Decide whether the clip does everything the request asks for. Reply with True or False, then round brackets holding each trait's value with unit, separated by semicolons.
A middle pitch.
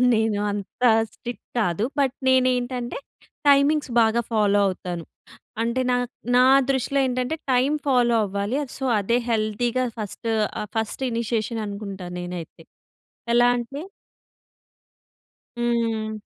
False (235 Hz)